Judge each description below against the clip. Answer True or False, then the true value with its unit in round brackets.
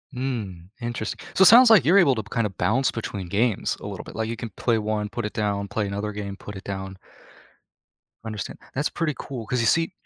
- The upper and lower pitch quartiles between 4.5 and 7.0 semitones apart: False (4.0 semitones)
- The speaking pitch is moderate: False (110 Hz)